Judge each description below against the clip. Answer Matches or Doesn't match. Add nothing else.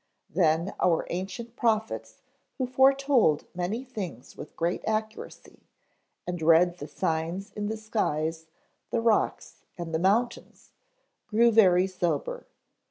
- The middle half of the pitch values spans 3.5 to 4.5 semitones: Doesn't match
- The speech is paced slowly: Matches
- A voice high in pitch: Matches